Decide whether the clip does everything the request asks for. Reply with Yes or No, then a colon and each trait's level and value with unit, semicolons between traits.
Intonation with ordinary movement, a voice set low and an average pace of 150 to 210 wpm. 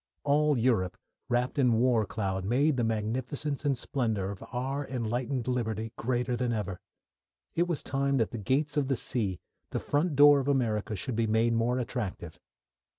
Yes: average, 3.7 semitones; low, 125 Hz; average, 170 wpm